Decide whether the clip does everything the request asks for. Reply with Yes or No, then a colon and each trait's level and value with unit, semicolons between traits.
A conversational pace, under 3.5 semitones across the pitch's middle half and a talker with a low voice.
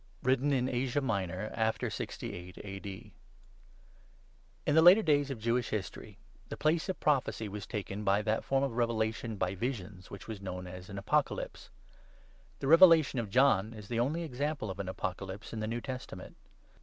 No: average, 180 wpm; wide, 5.5 semitones; low, 115 Hz